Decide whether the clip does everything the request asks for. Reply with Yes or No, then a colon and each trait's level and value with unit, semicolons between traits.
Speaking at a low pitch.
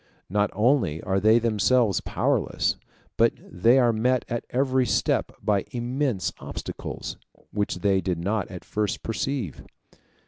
Yes: low, 110 Hz